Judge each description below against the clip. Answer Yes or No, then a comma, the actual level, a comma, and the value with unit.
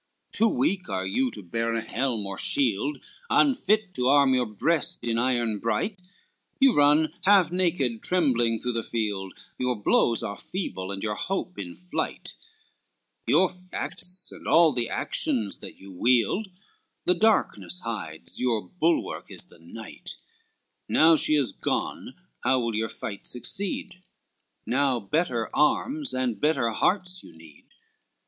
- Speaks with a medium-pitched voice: No, low, 125 Hz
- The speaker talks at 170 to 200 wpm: No, average, 150 wpm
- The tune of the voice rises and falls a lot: Yes, wide, 8.2 semitones